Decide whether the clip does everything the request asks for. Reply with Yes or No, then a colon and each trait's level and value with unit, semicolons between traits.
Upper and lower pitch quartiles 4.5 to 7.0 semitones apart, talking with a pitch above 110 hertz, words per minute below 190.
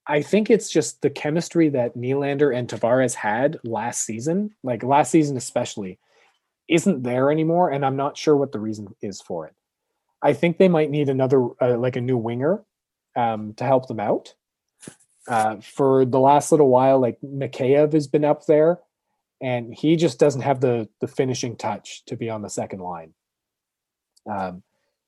No: average, 3.9 semitones; low, 135 Hz; average, 175 wpm